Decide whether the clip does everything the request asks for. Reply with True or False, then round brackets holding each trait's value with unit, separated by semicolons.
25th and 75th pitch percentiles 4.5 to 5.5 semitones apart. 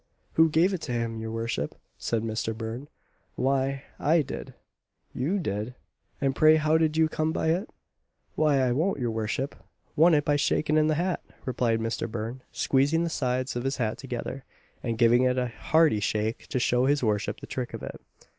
True (5.1 semitones)